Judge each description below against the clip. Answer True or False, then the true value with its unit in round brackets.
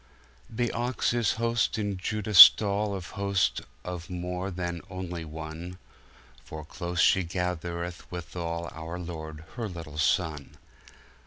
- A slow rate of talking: True (110 wpm)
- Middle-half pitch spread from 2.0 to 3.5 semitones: True (3.0 semitones)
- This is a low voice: True (90 Hz)